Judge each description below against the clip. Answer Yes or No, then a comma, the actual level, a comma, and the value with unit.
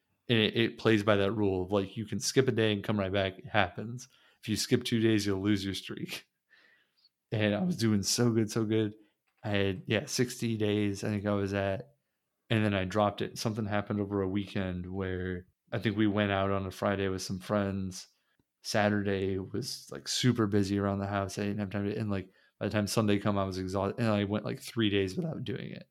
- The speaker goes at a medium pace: No, fast, 235 wpm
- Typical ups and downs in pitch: No, narrow, 2.1 semitones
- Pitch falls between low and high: No, low, 105 Hz